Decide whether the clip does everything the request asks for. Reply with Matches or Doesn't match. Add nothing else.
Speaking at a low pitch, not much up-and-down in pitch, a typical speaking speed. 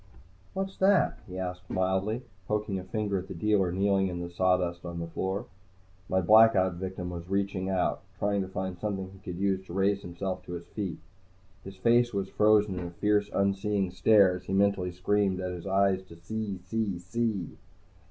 Matches